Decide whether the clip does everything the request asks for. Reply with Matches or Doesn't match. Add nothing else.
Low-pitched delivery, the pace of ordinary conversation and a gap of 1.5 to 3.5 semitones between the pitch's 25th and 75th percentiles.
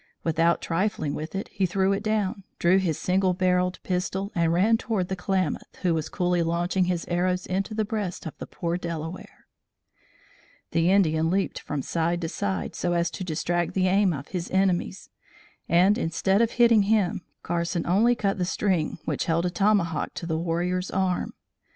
Doesn't match